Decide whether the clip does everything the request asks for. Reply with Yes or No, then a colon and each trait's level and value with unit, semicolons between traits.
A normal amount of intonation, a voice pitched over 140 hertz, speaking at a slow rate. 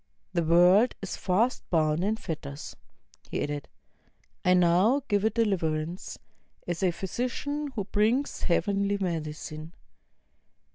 Yes: average, 4.6 semitones; medium, 185 Hz; slow, 115 wpm